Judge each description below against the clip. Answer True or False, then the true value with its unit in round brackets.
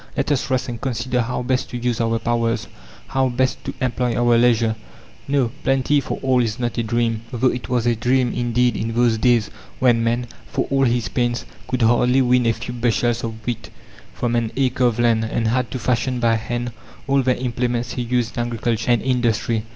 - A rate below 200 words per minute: False (205 wpm)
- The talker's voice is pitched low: True (120 Hz)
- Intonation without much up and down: True (1.4 semitones)